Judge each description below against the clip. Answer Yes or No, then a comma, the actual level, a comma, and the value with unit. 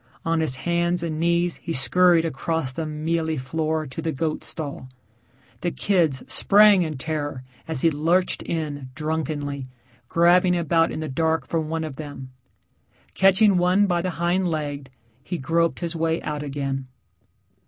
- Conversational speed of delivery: Yes, average, 155 wpm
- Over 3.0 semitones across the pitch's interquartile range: No, average, 2.7 semitones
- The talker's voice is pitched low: No, medium, 160 Hz